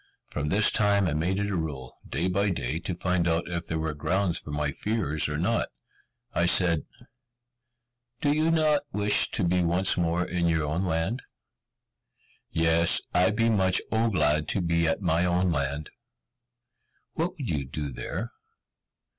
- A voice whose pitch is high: No, very low, 85 Hz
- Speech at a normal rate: Yes, average, 170 wpm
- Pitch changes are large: No, average, 3.9 semitones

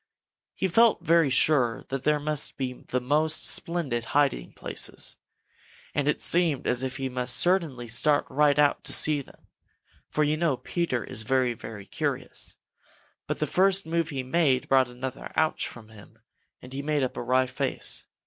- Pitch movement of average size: Yes, average, 3.5 semitones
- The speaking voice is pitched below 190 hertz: Yes, medium, 140 Hz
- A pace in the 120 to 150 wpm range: No, average, 170 wpm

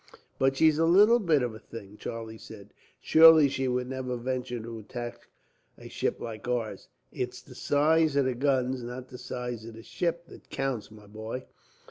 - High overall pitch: No, low, 125 Hz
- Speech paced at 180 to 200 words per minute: Yes, average, 185 wpm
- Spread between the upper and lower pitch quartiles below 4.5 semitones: Yes, average, 3.6 semitones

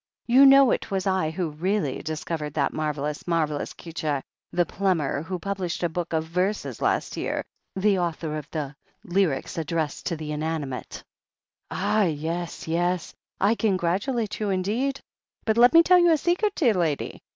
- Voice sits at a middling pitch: Yes, medium, 175 Hz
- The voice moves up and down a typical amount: Yes, average, 4.7 semitones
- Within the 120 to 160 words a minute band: No, average, 170 wpm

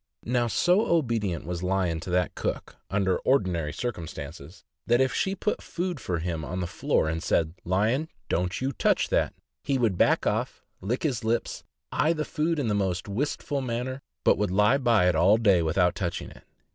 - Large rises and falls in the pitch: Yes, wide, 6.7 semitones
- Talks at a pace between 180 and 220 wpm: Yes, average, 190 wpm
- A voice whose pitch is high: No, low, 105 Hz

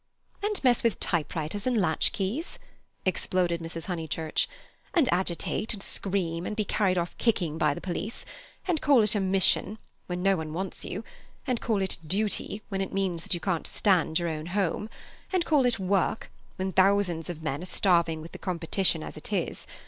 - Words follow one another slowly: No, average, 180 wpm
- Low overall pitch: No, high, 190 Hz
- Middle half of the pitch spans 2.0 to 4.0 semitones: Yes, average, 3.7 semitones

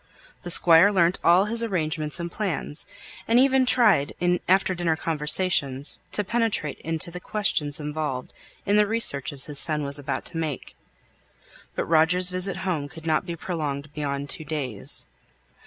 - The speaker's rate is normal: Yes, average, 155 wpm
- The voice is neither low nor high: Yes, medium, 165 Hz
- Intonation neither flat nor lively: Yes, average, 4.0 semitones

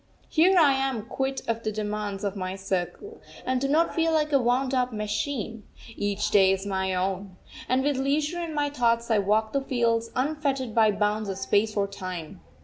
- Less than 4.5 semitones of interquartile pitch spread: No, average, 5.1 semitones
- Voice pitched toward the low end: No, high, 230 Hz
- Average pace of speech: Yes, average, 195 wpm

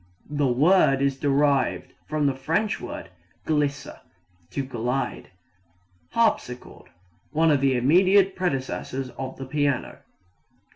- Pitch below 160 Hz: Yes, medium, 140 Hz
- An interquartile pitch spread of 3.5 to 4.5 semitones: No, average, 2.9 semitones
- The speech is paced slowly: Yes, slow, 110 wpm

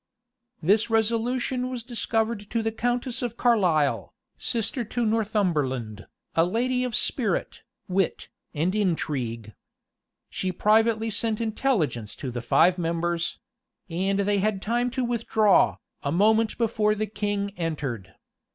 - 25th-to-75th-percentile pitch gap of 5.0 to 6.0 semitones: Yes, average, 5.3 semitones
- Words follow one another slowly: Yes, slow, 125 wpm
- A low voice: No, high, 210 Hz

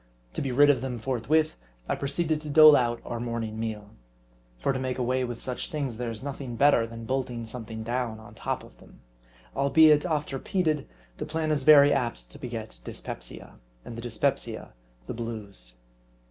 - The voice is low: Yes, low, 125 Hz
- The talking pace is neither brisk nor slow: Yes, average, 180 wpm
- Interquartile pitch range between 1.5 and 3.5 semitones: No, average, 4.0 semitones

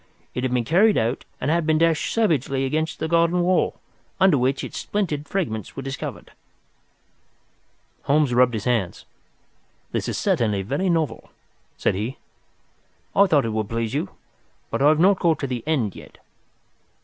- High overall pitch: No, medium, 140 Hz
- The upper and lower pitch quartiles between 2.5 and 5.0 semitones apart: No, wide, 5.6 semitones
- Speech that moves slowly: No, average, 170 wpm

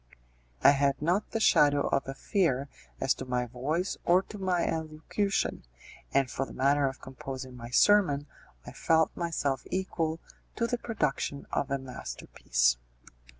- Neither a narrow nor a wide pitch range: Yes, average, 4.8 semitones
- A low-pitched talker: No, medium, 145 Hz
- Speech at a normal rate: Yes, average, 150 wpm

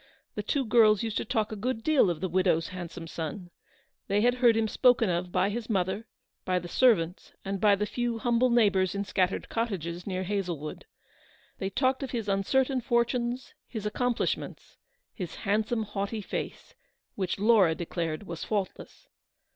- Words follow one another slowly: No, average, 170 wpm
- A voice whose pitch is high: Yes, high, 205 Hz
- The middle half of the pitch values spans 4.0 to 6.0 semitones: Yes, average, 4.3 semitones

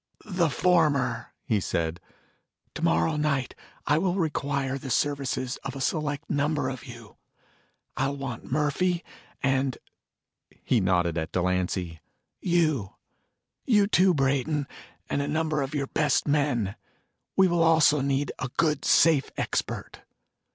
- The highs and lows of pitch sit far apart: No, average, 3.6 semitones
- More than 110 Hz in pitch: Yes, medium, 140 Hz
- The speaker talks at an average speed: No, slow, 130 wpm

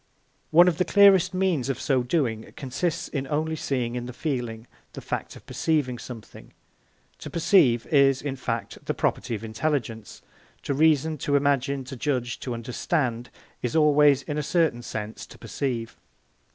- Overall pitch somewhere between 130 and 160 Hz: Yes, low, 135 Hz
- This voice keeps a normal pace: Yes, average, 165 wpm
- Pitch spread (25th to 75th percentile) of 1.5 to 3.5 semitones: No, average, 4.4 semitones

